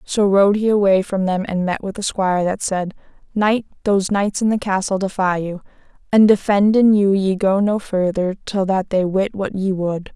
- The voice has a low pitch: No, high, 195 Hz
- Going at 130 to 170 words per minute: No, fast, 205 wpm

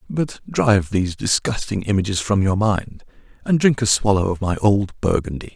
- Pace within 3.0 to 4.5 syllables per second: No, 5.1 syllables/s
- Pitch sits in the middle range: No, low, 105 Hz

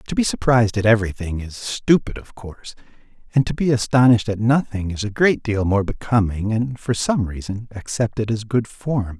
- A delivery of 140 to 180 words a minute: No, average, 190 wpm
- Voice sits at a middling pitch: No, low, 110 Hz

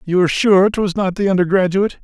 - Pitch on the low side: No, high, 190 Hz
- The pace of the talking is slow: No, fast, 205 wpm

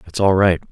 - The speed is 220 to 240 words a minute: No, fast, 250 wpm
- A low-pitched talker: Yes, very low, 90 Hz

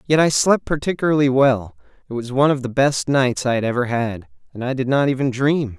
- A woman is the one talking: No, male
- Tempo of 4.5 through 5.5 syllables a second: No, 5.7 syllables/s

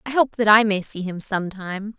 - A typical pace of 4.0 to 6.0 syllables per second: Yes, 5.9 syllables/s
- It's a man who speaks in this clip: No, female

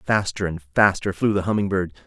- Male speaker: Yes, male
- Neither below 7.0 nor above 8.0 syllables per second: No, 5.6 syllables/s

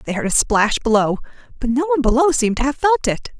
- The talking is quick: Yes, fast, 250 wpm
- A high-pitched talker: Yes, very high, 260 Hz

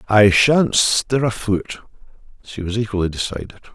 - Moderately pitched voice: No, low, 110 Hz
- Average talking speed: Yes, average, 145 wpm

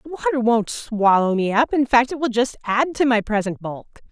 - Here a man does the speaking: No, female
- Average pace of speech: No, fast, 235 wpm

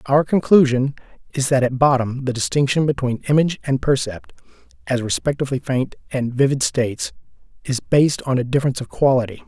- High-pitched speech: No, low, 135 Hz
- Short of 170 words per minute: Yes, average, 160 wpm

